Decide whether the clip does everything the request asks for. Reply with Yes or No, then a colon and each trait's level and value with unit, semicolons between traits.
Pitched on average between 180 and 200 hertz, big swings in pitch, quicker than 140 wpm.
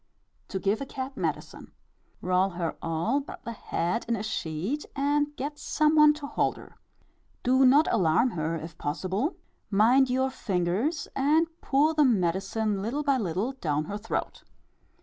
No: high, 230 Hz; wide, 7.4 semitones; average, 160 wpm